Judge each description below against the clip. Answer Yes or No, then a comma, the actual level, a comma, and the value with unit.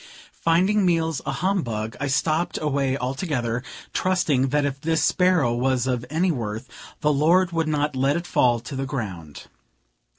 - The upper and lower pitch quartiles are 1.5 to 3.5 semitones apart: No, average, 4.6 semitones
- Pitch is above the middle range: No, medium, 145 Hz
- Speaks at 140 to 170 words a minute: Yes, average, 160 wpm